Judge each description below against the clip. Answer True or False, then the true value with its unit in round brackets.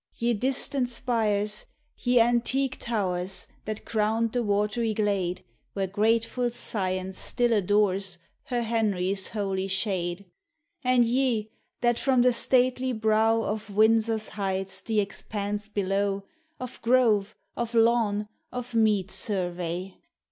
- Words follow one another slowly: True (120 wpm)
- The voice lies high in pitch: True (215 Hz)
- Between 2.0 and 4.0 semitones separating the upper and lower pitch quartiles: True (3.1 semitones)